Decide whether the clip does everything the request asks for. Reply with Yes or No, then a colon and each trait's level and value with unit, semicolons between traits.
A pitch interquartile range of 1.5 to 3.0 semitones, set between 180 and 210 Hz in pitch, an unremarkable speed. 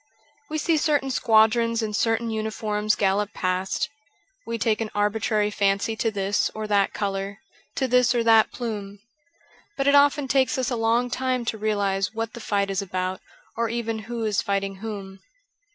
No: average, 2.7 semitones; high, 220 Hz; average, 170 wpm